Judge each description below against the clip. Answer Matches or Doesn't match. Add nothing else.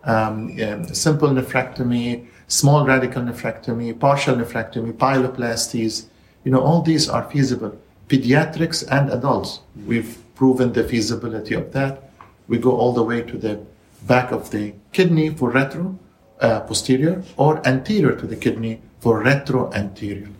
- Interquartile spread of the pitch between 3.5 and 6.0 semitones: Doesn't match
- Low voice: Matches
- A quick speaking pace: Doesn't match